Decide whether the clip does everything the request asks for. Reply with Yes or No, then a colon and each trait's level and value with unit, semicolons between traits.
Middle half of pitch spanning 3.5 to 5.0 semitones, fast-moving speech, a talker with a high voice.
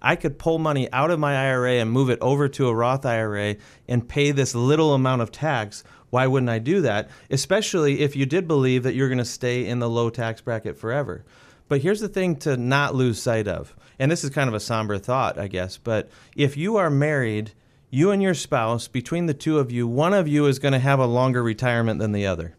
No: average, 3.9 semitones; fast, 240 wpm; low, 130 Hz